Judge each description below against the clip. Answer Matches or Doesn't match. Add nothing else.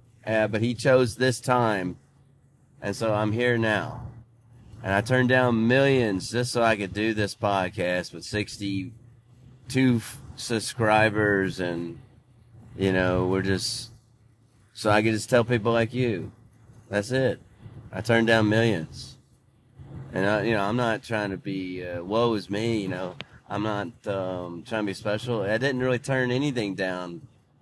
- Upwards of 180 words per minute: Doesn't match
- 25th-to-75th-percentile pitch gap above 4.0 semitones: Doesn't match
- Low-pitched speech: Matches